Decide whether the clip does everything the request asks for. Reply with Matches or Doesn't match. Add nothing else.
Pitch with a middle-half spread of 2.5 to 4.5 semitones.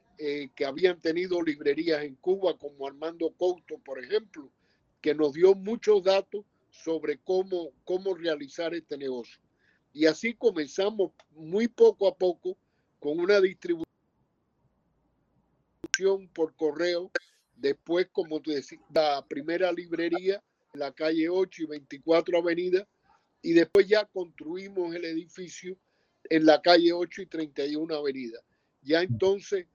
Matches